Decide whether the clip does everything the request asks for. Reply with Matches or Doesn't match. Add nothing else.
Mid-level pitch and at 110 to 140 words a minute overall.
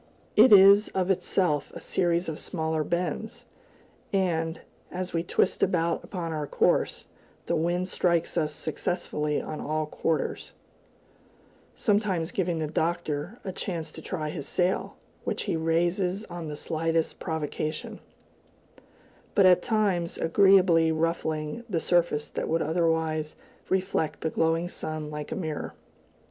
Matches